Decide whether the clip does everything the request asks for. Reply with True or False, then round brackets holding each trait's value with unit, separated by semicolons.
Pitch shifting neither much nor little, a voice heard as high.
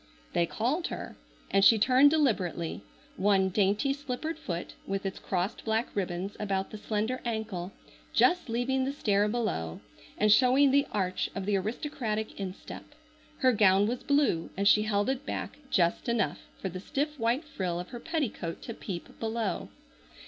True (4.9 semitones; 215 Hz)